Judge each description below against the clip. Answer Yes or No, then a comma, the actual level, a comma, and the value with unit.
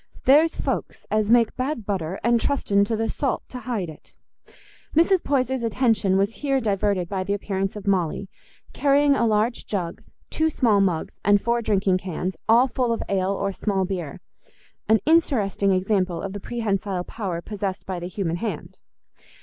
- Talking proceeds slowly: No, average, 165 wpm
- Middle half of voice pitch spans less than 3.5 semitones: No, average, 3.8 semitones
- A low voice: No, high, 205 Hz